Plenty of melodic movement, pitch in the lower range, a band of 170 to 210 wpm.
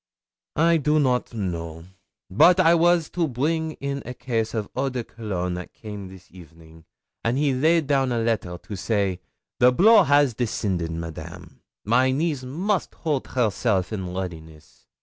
No: wide, 7.6 semitones; low, 120 Hz; average, 160 wpm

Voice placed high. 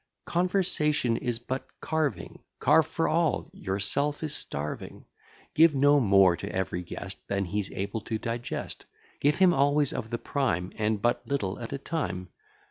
No: low, 120 Hz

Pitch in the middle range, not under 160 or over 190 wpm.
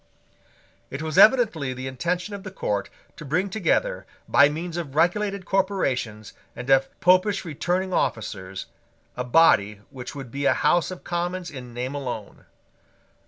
No: medium, 155 Hz; average, 150 wpm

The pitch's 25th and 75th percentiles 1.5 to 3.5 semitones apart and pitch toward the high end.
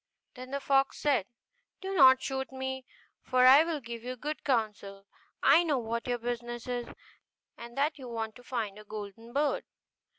Yes: average, 2.8 semitones; very high, 250 Hz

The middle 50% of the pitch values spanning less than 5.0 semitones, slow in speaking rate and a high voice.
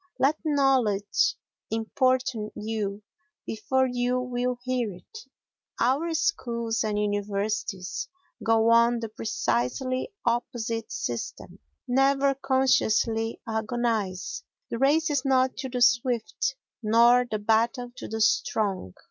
Yes: average, 3.0 semitones; slow, 110 wpm; high, 235 Hz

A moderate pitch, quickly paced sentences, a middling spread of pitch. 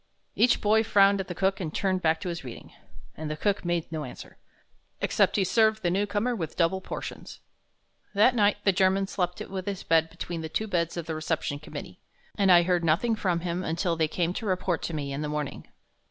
Yes: medium, 180 Hz; fast, 220 wpm; average, 3.5 semitones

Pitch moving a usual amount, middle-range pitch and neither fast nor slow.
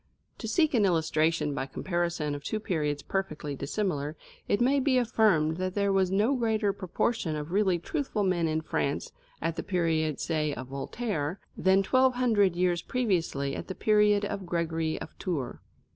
Yes: average, 5.0 semitones; medium, 180 Hz; average, 170 wpm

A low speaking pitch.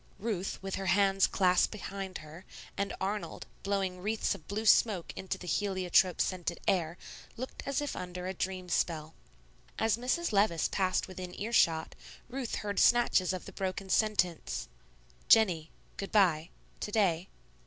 No: high, 190 Hz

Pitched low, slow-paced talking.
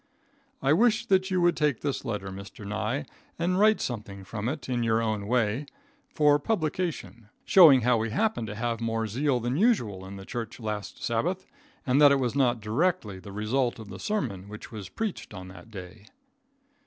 No: low, 120 Hz; average, 190 wpm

